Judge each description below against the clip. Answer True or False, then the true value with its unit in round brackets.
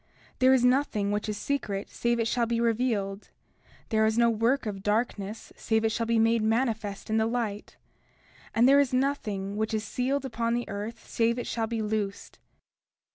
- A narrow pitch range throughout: True (2.2 semitones)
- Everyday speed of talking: True (190 wpm)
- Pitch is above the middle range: True (225 Hz)